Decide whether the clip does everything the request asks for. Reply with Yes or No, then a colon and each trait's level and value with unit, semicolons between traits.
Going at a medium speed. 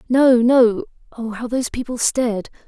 Yes: average, 155 wpm